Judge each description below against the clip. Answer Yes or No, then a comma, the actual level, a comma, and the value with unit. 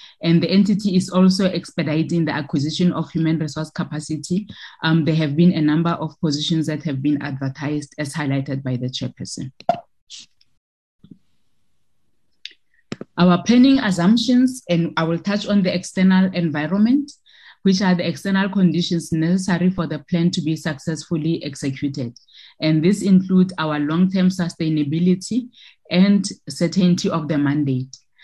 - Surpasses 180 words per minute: No, average, 140 wpm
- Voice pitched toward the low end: No, medium, 170 Hz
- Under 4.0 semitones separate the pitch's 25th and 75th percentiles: Yes, average, 3.5 semitones